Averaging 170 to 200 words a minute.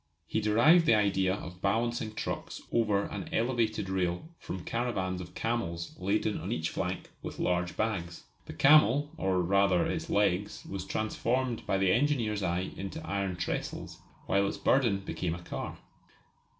No: average, 155 wpm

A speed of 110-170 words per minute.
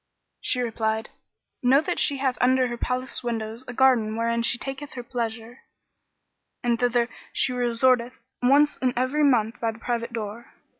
Yes: average, 165 wpm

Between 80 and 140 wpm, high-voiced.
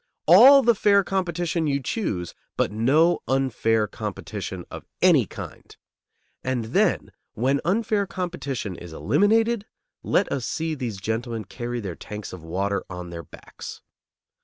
No: slow, 135 wpm; low, 130 Hz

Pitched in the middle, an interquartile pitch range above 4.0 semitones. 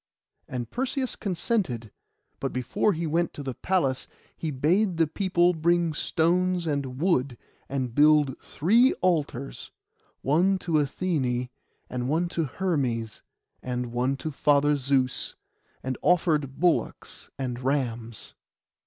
Yes: medium, 150 Hz; average, 5.2 semitones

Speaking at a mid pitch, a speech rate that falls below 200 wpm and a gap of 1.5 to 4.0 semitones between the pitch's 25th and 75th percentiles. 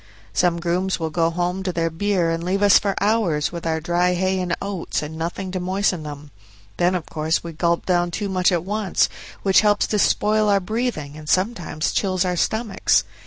No: medium, 180 Hz; fast, 205 wpm; average, 2.9 semitones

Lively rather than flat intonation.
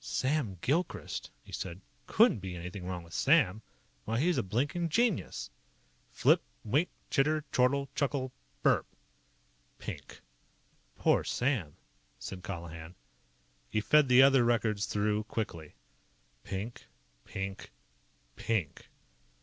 Yes: wide, 7.0 semitones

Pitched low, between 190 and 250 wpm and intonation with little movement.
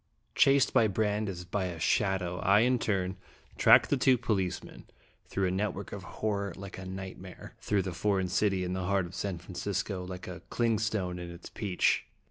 Yes: very low, 95 Hz; average, 195 wpm; narrow, 2.3 semitones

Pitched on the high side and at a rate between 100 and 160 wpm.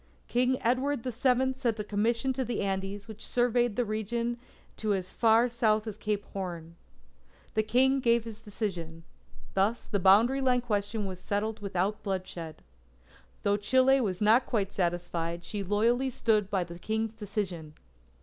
Yes: high, 215 Hz; average, 155 wpm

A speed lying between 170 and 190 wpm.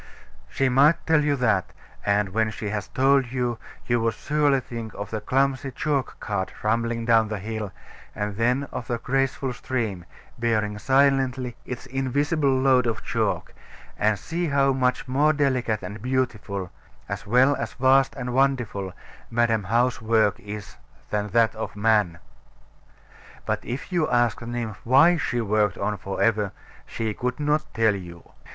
No: average, 160 wpm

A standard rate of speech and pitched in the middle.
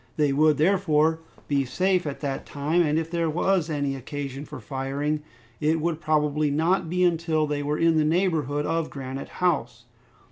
Yes: average, 175 wpm; medium, 155 Hz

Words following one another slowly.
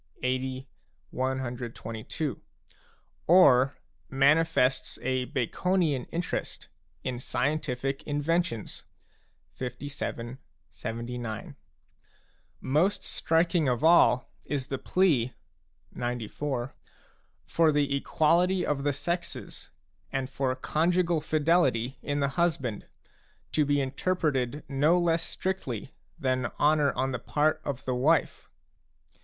Yes: slow, 100 wpm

